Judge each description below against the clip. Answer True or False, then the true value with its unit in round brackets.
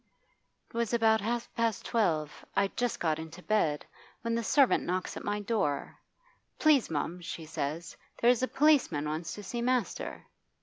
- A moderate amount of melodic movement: False (6.4 semitones)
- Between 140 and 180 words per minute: True (165 wpm)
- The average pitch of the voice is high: True (205 Hz)